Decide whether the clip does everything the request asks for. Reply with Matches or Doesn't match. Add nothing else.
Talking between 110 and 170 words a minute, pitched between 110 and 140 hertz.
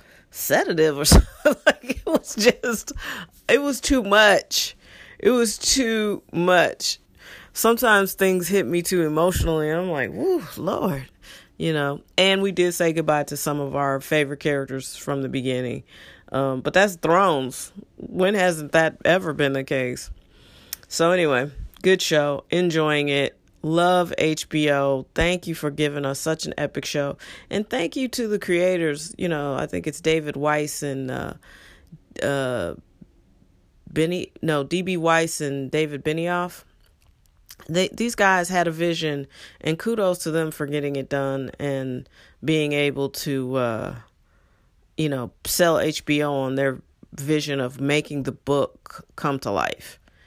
Doesn't match